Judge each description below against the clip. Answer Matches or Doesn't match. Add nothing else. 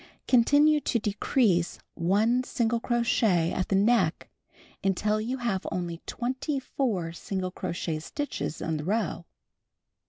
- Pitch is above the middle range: Matches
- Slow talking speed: Matches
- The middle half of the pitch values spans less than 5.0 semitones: Doesn't match